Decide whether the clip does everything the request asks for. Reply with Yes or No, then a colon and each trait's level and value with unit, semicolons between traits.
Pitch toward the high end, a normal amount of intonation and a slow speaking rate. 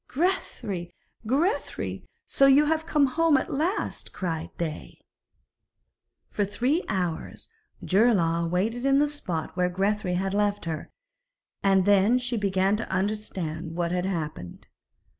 No: high, 200 Hz; wide, 6.4 semitones; slow, 130 wpm